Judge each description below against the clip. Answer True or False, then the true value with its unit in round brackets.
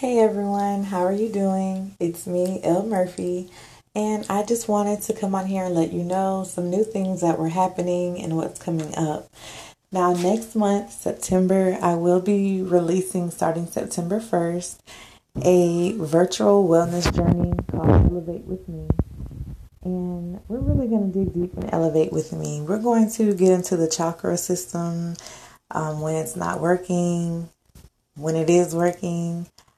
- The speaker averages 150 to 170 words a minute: True (160 wpm)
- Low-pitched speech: False (180 Hz)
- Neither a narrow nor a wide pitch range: False (2.3 semitones)